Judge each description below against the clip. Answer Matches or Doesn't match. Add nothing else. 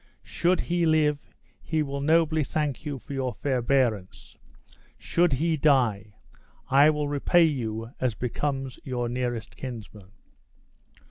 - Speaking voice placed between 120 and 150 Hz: Matches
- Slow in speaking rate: Matches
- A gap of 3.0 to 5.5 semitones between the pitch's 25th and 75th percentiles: Matches